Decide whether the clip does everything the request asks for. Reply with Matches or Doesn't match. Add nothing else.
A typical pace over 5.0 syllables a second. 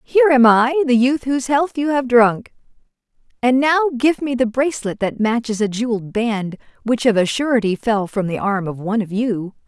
Matches